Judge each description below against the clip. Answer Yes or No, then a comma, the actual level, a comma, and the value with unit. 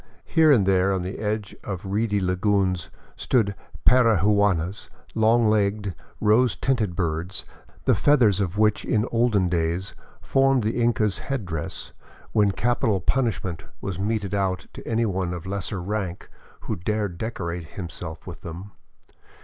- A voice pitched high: No, low, 100 Hz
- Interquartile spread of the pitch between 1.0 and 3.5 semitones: Yes, average, 3.2 semitones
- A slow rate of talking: No, average, 145 wpm